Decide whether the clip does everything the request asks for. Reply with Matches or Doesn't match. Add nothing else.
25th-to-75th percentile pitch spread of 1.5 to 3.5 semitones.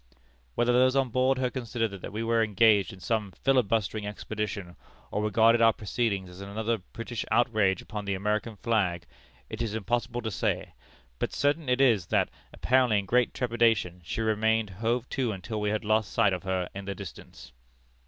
Matches